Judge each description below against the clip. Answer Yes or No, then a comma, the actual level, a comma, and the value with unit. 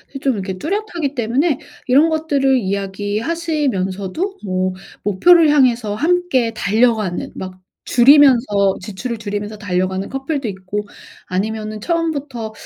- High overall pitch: Yes, high, 230 Hz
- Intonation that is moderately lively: No, wide, 6.5 semitones